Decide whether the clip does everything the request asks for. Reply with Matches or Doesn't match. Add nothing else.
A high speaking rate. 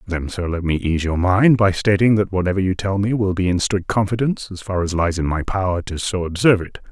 Matches